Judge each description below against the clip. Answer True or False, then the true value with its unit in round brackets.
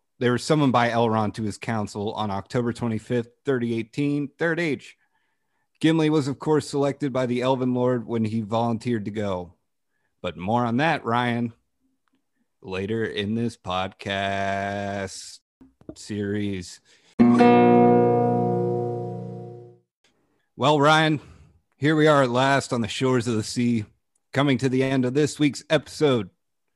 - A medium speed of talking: False (130 wpm)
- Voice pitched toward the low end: True (120 Hz)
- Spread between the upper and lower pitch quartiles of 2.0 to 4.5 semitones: False (5.5 semitones)